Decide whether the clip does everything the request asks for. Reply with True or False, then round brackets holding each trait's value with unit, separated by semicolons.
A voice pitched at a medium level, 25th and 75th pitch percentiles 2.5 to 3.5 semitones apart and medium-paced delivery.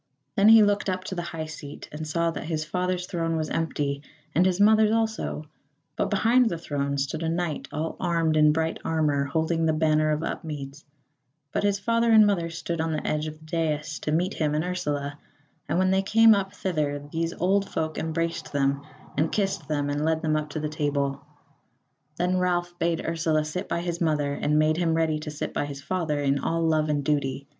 False (160 Hz; 2.8 semitones; 210 wpm)